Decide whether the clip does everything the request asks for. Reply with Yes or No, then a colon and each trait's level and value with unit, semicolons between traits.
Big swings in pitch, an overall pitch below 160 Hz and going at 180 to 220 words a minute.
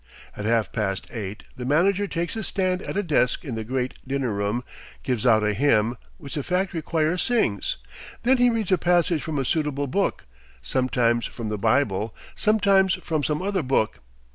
Yes: wide, 7.8 semitones; medium, 140 Hz; average, 185 wpm